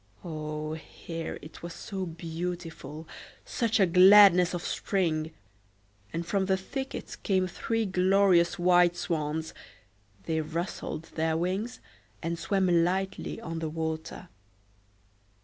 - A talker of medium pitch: Yes, medium, 175 Hz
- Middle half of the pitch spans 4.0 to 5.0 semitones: No, average, 2.9 semitones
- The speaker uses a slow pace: Yes, slow, 115 wpm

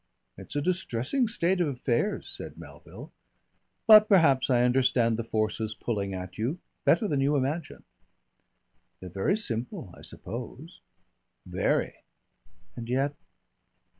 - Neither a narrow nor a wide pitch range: No, wide, 6.6 semitones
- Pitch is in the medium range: No, low, 130 Hz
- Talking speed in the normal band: No, slow, 125 wpm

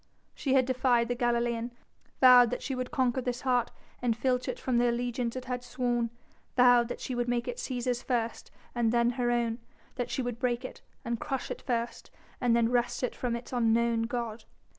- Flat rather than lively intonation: Yes, narrow, 1.0 semitones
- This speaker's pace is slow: No, fast, 205 wpm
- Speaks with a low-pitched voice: No, high, 245 Hz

